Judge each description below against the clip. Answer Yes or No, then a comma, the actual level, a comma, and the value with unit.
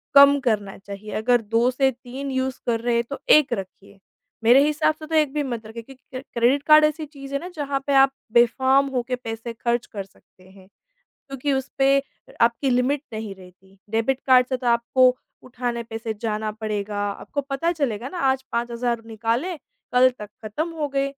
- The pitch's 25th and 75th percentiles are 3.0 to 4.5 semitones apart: Yes, average, 3.6 semitones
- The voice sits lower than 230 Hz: No, very high, 250 Hz